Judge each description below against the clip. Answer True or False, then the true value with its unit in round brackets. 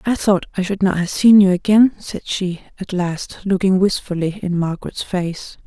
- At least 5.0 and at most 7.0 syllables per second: False (4.8 syllables/s)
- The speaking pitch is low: False (190 Hz)